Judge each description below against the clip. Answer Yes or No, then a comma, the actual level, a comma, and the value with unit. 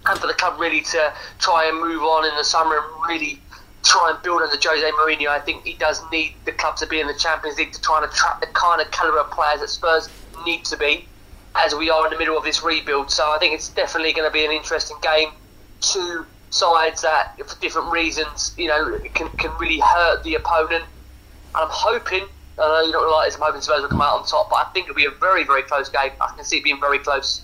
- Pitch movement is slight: Yes, narrow, 1.4 semitones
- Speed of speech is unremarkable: No, fast, 255 wpm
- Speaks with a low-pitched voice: No, medium, 155 Hz